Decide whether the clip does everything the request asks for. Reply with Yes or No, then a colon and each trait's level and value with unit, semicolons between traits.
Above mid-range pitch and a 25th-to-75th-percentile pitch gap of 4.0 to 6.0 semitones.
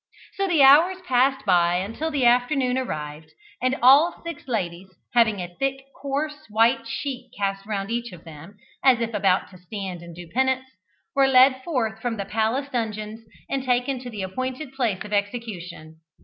Yes: high, 235 Hz; average, 5.2 semitones